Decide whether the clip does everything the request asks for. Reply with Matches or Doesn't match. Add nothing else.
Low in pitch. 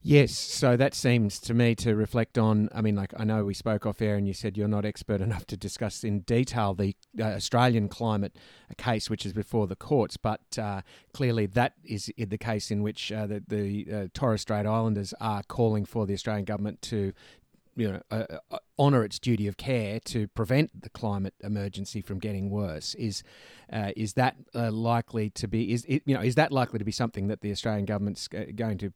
Matches